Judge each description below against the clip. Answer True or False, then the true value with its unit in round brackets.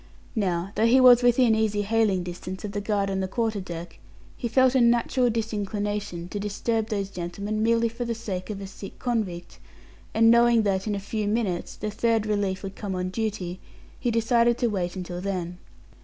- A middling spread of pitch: True (3.2 semitones)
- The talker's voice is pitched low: False (210 Hz)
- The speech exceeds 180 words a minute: True (195 wpm)